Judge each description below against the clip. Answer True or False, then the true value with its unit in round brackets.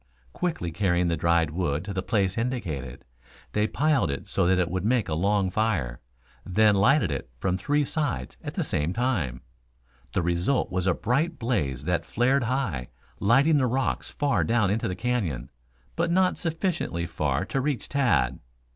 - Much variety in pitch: True (7.4 semitones)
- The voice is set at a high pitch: False (100 Hz)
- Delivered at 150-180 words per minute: True (175 wpm)